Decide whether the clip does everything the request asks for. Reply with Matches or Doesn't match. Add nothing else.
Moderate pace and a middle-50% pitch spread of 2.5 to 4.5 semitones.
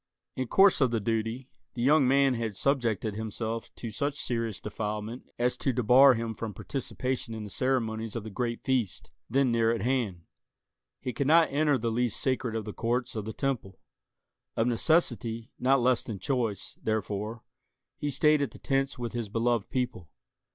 Matches